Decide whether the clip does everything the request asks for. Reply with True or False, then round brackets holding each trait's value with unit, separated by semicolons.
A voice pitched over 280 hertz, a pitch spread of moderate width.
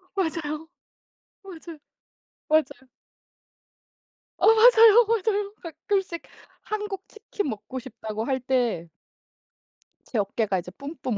False (320 Hz; 8.5 semitones)